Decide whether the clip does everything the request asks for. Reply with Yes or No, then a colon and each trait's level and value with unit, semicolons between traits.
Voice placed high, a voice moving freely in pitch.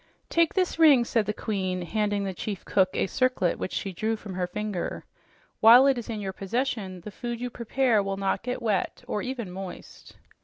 No: high, 210 Hz; average, 4.0 semitones